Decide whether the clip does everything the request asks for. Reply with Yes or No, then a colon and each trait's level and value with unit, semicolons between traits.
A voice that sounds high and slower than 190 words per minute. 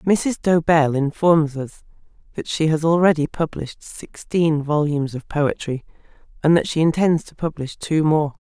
No: medium, 155 Hz; average, 150 wpm